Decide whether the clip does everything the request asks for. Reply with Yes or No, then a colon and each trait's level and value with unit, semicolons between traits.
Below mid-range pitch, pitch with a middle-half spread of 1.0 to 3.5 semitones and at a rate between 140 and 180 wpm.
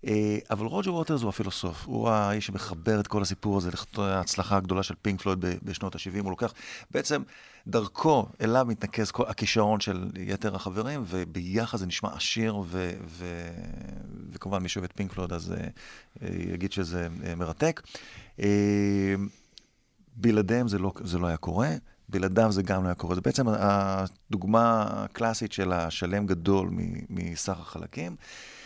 Yes: low, 100 Hz; average, 2.8 semitones; fast, 150 wpm